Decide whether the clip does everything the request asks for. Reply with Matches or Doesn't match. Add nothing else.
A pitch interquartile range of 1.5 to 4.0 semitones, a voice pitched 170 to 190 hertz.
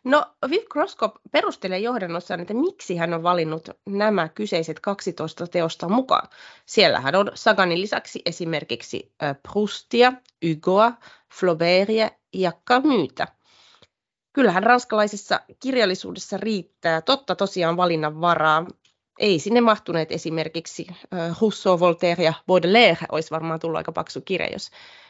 Doesn't match